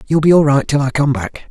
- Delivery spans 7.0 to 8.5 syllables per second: Yes, 7.1 syllables/s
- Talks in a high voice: No, medium, 140 Hz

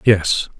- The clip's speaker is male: Yes, male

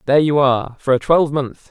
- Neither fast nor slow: No, fast, 210 wpm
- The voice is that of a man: Yes, male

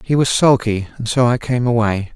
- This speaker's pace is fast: Yes, fast, 225 wpm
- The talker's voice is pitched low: Yes, low, 120 Hz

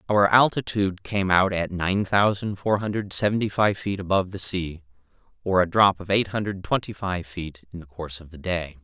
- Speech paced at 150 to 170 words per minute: No, fast, 205 wpm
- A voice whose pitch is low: Yes, very low, 95 Hz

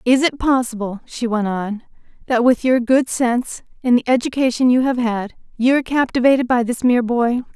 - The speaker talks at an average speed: Yes, average, 190 wpm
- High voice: Yes, high, 245 Hz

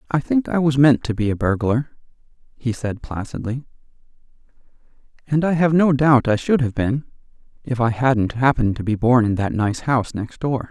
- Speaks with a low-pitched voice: Yes, low, 125 Hz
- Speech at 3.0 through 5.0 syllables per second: No, 5.2 syllables/s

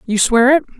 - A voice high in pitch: Yes, very high, 250 Hz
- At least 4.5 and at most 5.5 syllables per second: No, 5.7 syllables/s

